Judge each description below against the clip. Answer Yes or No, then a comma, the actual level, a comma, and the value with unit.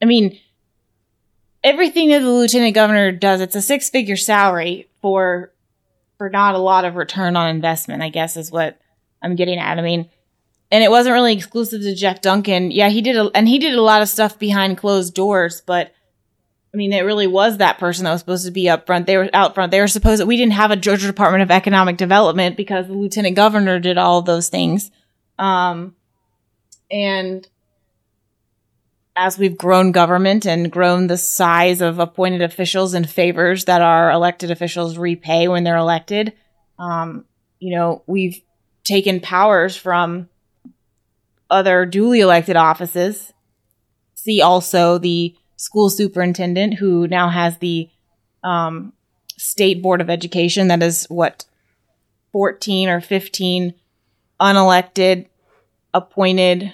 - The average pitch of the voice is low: No, medium, 180 Hz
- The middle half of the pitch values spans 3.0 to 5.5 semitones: No, narrow, 2.6 semitones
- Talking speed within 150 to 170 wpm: Yes, average, 160 wpm